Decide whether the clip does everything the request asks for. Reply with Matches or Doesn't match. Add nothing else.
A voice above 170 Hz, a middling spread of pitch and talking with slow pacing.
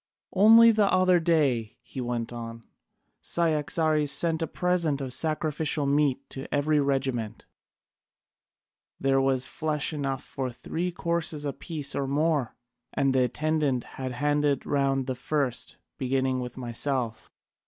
Doesn't match